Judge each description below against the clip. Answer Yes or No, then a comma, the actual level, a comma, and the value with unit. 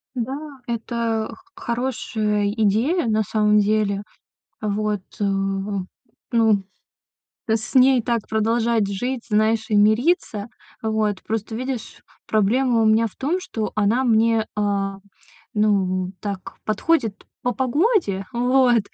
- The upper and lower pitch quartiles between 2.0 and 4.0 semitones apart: Yes, average, 2.7 semitones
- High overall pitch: Yes, high, 220 Hz